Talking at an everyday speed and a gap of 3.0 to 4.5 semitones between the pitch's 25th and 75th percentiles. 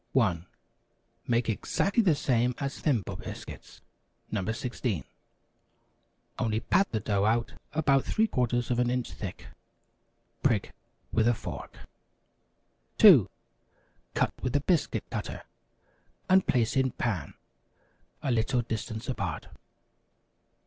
No: slow, 115 wpm; average, 3.5 semitones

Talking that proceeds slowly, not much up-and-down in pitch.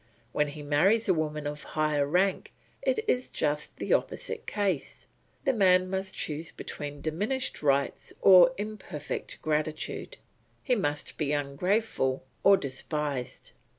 No: slow, 130 wpm; average, 5.2 semitones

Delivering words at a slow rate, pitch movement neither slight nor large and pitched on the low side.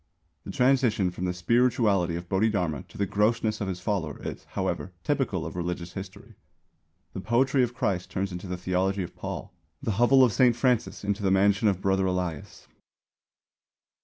No: average, 170 wpm; average, 4.3 semitones; low, 100 Hz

